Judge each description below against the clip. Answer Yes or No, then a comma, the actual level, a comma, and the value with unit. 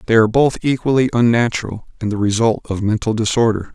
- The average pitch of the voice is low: Yes, low, 115 Hz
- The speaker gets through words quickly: No, average, 175 wpm